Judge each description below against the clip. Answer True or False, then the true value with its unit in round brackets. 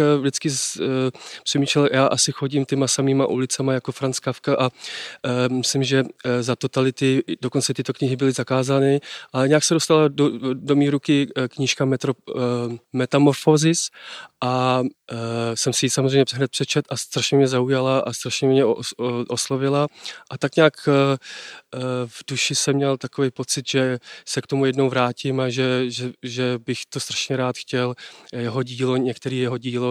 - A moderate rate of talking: False (175 wpm)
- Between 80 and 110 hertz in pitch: False (135 Hz)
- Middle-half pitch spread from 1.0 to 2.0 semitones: True (1.7 semitones)